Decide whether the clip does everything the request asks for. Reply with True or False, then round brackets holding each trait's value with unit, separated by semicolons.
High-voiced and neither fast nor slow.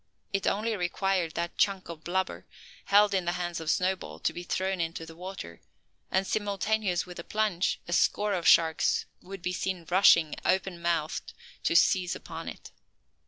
False (180 Hz; 170 wpm)